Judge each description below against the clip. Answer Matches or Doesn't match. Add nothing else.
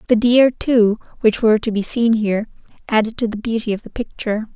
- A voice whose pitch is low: Doesn't match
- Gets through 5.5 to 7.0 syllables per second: Matches